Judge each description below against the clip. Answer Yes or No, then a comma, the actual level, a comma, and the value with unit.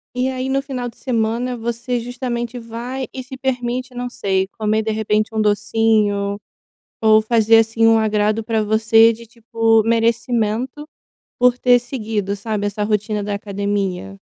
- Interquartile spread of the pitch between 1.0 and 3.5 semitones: Yes, narrow, 2.4 semitones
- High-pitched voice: Yes, high, 225 Hz